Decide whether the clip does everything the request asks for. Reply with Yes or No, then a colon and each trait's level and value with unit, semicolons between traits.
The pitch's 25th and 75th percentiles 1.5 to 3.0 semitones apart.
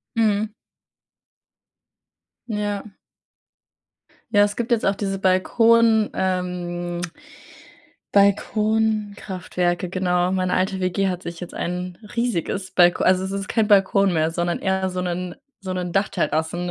Yes: narrow, 2.4 semitones